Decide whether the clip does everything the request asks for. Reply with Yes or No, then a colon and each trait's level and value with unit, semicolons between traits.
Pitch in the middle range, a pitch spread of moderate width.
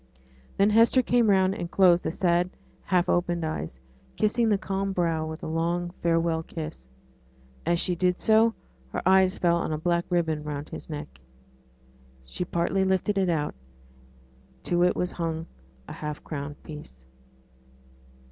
Yes: medium, 175 Hz; average, 3.0 semitones